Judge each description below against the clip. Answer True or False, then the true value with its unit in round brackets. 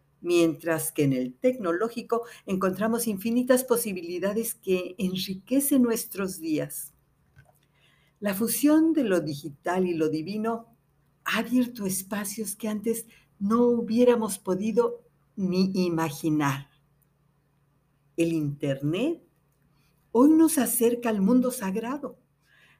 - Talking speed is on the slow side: True (100 wpm)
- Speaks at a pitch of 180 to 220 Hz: True (190 Hz)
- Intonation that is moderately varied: False (7.0 semitones)